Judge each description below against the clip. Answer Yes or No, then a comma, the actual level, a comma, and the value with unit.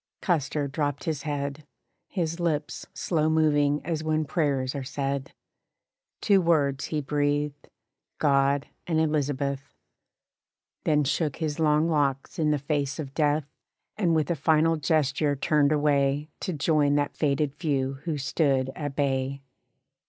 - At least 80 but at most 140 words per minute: Yes, slow, 135 wpm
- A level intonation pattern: Yes, narrow, 2.0 semitones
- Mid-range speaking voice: Yes, medium, 145 Hz